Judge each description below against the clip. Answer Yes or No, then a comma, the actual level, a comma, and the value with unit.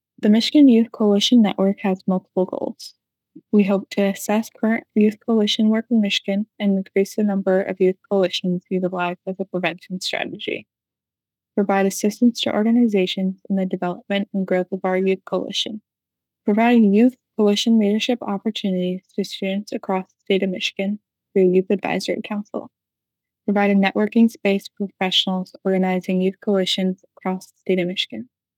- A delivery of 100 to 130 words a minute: No, average, 155 wpm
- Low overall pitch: No, high, 195 Hz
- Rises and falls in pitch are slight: Yes, narrow, 2.3 semitones